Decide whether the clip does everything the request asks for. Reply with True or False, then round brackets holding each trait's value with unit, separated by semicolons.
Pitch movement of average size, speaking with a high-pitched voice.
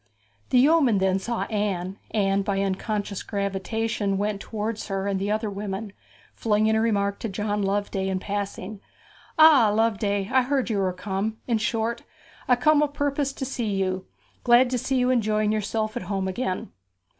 True (3.1 semitones; 210 Hz)